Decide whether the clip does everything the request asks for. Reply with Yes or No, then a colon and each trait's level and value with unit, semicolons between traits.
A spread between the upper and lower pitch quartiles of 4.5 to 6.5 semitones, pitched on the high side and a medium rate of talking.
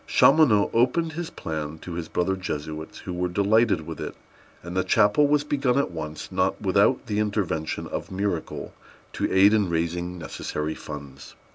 No: average, 5.1 semitones; very low, 95 Hz; average, 170 wpm